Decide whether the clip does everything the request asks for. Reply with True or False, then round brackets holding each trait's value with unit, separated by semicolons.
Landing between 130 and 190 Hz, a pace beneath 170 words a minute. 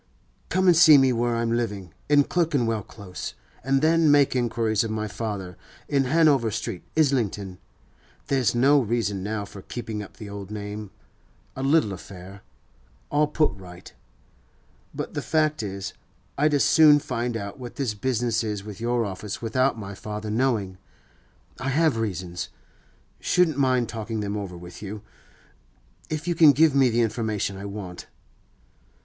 False (115 Hz; 155 wpm)